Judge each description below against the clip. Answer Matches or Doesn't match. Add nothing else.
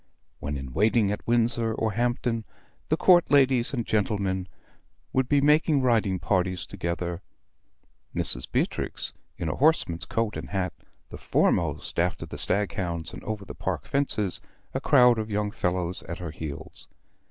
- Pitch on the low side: Matches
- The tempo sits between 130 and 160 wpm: Matches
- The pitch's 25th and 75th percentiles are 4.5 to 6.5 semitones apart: Matches